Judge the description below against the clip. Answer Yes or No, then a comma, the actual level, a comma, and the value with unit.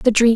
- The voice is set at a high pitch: Yes, high, 230 Hz